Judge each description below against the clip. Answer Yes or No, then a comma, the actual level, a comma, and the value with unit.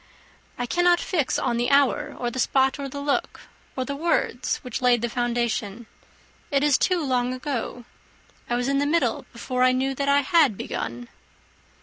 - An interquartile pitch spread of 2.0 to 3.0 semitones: Yes, average, 2.7 semitones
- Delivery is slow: No, average, 185 wpm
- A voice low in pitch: No, very high, 260 Hz